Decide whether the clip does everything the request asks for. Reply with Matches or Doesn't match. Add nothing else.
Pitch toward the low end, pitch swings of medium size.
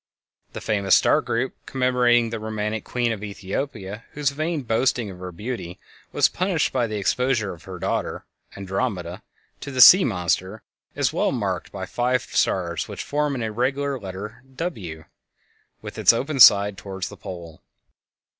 Matches